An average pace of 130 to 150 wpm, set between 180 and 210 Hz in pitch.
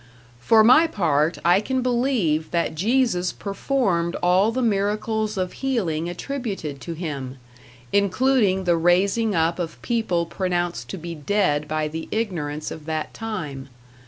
Yes: average, 140 wpm; medium, 185 Hz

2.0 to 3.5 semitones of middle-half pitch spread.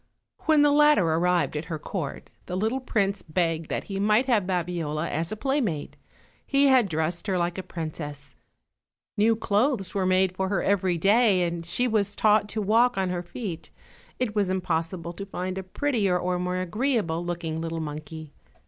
No: average, 4.1 semitones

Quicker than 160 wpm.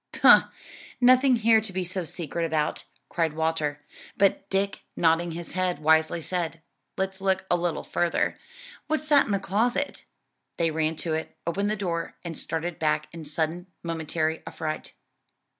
No: average, 155 wpm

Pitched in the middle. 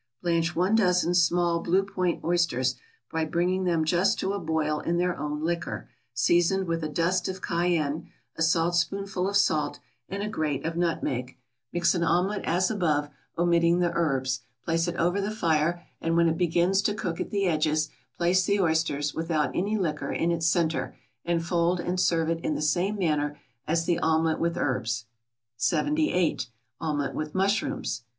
Yes: medium, 170 Hz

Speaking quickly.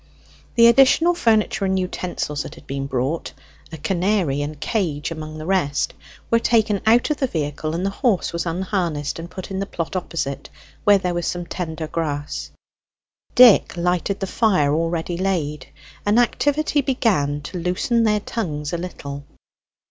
No: average, 165 wpm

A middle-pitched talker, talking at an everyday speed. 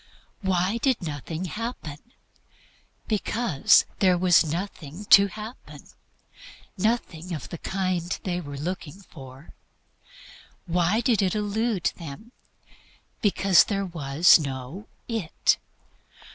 No: medium, 180 Hz; slow, 105 wpm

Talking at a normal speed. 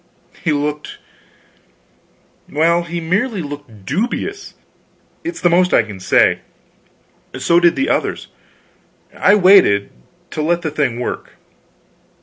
No: slow, 120 wpm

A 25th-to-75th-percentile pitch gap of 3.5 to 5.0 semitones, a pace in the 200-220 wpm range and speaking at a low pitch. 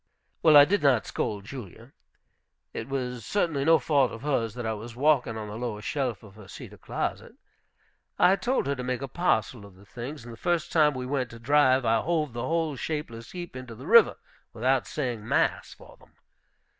Yes: average, 4.5 semitones; fast, 205 wpm; low, 130 Hz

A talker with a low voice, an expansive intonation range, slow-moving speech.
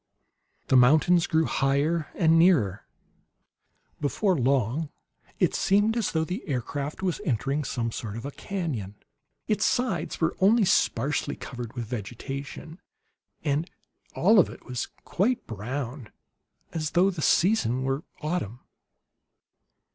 No: medium, 150 Hz; wide, 6.1 semitones; slow, 125 wpm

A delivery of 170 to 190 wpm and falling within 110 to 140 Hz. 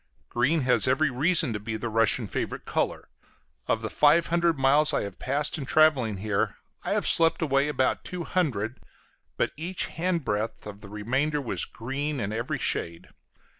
Yes: average, 175 wpm; low, 135 Hz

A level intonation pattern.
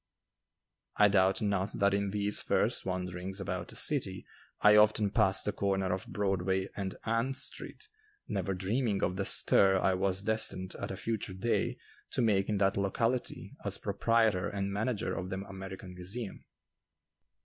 Yes: narrow, 2.0 semitones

